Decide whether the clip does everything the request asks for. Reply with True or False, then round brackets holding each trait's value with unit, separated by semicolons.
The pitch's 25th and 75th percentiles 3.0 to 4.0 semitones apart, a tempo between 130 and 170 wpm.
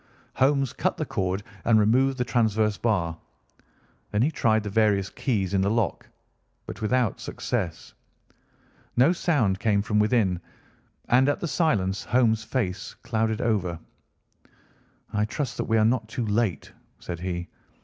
True (3.7 semitones; 150 wpm)